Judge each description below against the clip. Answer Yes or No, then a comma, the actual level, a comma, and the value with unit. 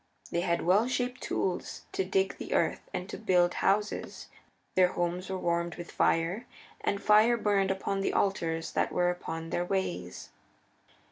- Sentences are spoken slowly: No, average, 160 wpm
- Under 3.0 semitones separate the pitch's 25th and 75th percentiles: Yes, narrow, 2.4 semitones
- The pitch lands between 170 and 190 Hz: Yes, medium, 185 Hz